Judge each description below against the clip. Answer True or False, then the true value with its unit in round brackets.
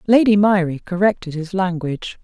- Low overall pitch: False (185 Hz)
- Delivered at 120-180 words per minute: True (135 wpm)